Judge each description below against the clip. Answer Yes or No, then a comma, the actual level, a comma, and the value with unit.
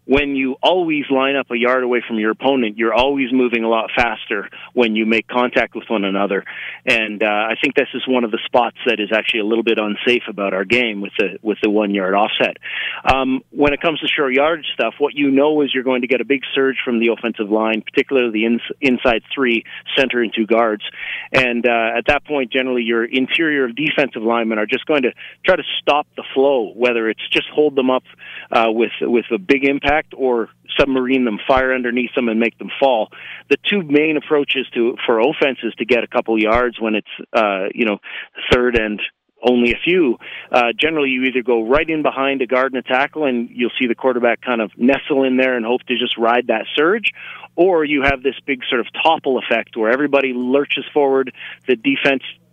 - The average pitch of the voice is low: Yes, low, 125 Hz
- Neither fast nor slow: No, fast, 215 wpm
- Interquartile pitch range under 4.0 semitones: Yes, average, 3.2 semitones